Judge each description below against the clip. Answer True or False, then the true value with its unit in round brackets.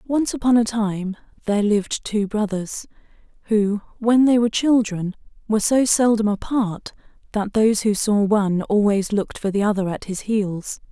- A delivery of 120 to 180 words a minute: True (165 wpm)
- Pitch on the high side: True (210 Hz)